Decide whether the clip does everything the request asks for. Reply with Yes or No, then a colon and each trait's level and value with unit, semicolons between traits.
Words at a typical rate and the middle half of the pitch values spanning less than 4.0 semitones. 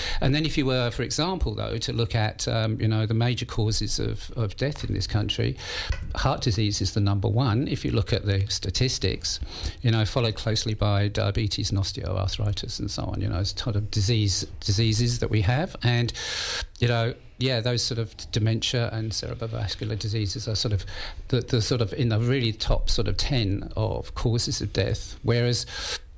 Yes: average, 195 wpm; average, 2.8 semitones